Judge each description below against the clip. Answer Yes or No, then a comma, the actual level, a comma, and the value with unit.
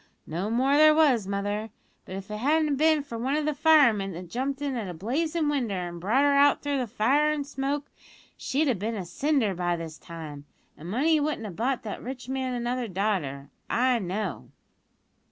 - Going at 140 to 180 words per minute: No, average, 195 wpm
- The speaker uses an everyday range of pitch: No, wide, 6.6 semitones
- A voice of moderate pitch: No, high, 245 Hz